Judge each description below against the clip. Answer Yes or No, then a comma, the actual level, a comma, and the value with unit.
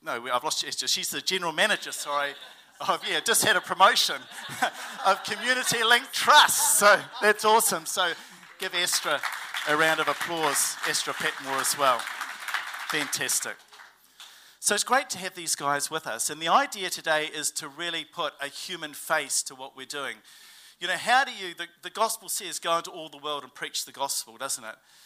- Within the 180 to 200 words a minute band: Yes, average, 185 wpm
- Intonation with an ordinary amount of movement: No, wide, 6.1 semitones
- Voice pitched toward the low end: No, medium, 170 Hz